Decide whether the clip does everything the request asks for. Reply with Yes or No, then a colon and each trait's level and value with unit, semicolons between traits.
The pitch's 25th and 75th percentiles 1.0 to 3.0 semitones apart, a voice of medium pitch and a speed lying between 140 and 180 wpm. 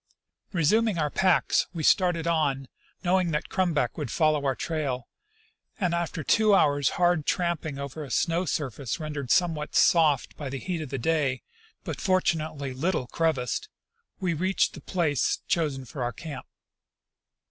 No: average, 3.8 semitones; medium, 155 Hz; average, 155 wpm